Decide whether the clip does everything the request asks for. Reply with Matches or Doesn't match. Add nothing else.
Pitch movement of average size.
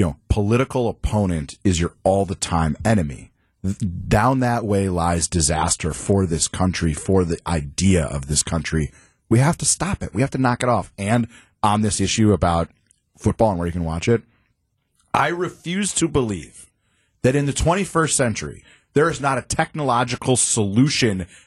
Doesn't match